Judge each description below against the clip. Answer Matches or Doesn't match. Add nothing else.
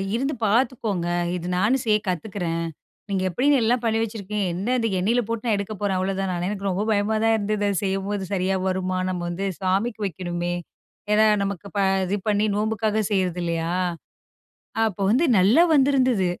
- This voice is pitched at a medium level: Doesn't match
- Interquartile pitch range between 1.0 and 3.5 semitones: Matches